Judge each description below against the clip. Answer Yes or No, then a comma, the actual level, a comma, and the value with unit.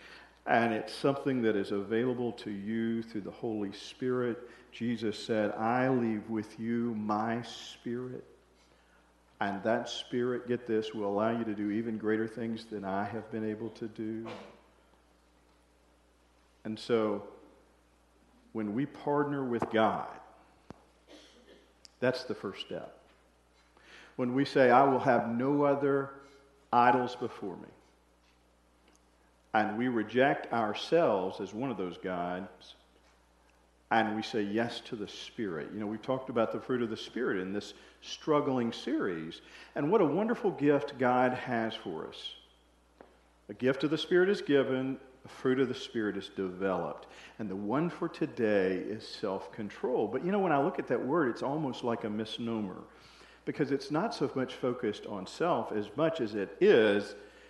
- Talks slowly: No, average, 155 wpm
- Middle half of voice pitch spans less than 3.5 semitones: No, average, 4.9 semitones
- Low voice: Yes, low, 110 Hz